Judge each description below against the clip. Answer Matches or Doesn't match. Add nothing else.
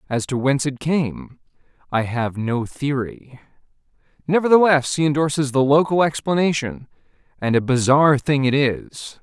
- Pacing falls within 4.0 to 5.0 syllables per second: Matches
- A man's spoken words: Matches